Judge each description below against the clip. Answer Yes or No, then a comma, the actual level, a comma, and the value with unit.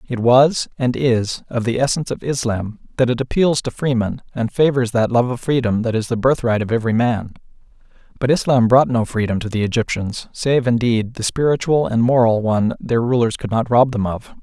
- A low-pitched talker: Yes, low, 120 Hz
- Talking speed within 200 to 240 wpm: Yes, fast, 205 wpm